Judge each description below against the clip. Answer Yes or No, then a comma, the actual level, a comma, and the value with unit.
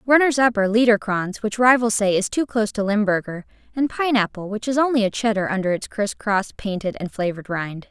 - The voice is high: Yes, high, 215 Hz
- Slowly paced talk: No, average, 195 wpm